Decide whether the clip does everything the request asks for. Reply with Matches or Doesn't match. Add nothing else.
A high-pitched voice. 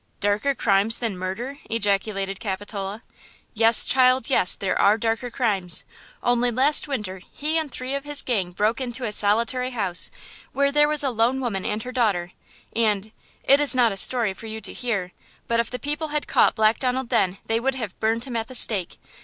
Matches